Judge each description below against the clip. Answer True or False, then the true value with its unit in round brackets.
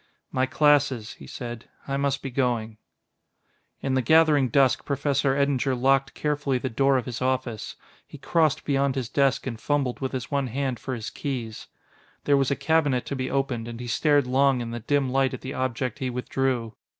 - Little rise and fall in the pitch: True (2.0 semitones)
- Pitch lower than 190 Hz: True (135 Hz)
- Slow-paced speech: False (195 wpm)